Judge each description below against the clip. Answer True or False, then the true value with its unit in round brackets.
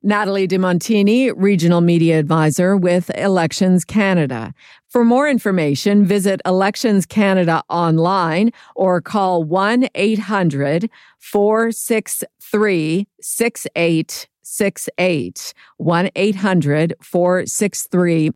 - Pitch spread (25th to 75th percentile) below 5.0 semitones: True (3.4 semitones)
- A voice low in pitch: False (190 Hz)